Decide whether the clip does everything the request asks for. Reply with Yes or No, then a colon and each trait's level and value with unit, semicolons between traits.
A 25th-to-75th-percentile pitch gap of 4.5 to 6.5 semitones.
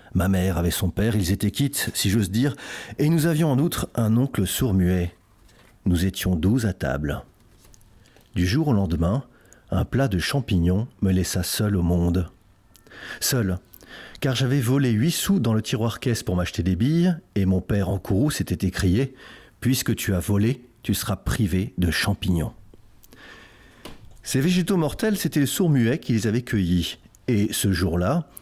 Yes: average, 5.2 semitones